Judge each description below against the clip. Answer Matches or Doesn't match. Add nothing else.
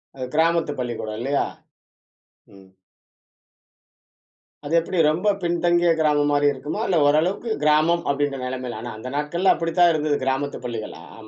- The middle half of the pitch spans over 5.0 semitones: Doesn't match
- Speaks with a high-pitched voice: Doesn't match